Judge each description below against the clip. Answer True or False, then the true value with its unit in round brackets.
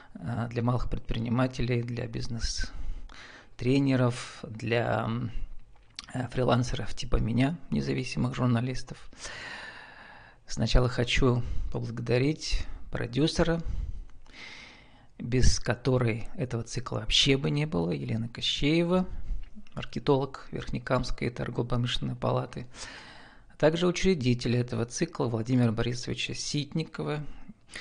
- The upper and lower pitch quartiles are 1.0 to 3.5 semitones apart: True (2.8 semitones)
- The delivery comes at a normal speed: False (80 wpm)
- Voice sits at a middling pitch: False (125 Hz)